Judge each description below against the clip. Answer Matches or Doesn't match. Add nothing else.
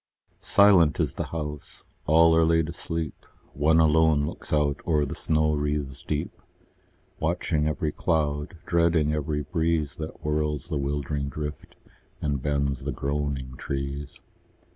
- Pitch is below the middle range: Matches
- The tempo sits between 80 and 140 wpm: Matches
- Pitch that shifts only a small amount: Matches